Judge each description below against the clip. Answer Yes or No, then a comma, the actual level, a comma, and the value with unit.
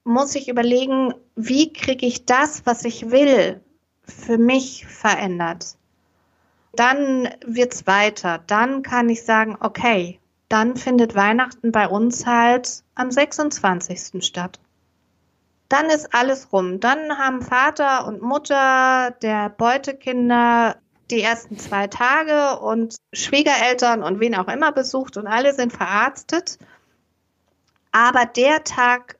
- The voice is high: Yes, high, 240 Hz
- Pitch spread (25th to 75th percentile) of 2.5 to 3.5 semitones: No, average, 4.0 semitones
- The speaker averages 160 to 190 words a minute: No, slow, 125 wpm